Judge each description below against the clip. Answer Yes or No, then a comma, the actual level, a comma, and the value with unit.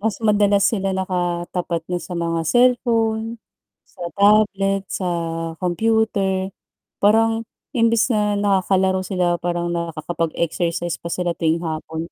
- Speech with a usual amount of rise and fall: Yes, average, 3.5 semitones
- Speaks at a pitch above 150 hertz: Yes, high, 190 Hz